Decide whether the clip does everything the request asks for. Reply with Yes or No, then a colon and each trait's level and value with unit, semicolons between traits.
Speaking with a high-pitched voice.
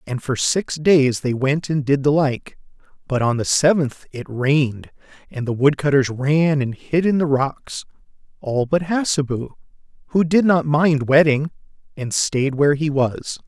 No: medium, 145 Hz